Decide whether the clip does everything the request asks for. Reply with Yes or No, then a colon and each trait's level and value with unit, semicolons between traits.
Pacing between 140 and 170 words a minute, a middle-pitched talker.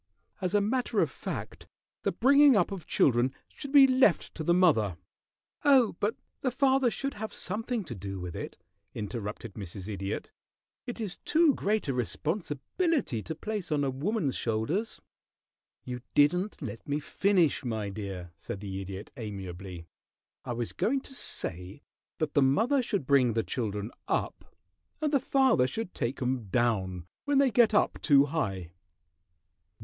Yes: average, 160 wpm; medium, 145 Hz